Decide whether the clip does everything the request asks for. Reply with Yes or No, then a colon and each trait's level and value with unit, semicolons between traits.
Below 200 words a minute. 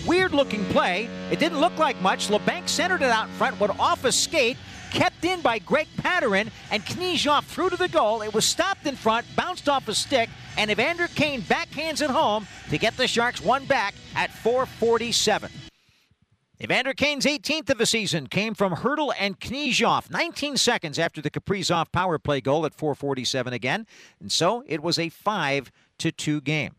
Yes: average, 180 wpm